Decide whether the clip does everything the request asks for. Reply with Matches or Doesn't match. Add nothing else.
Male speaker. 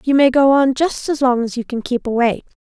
Doesn't match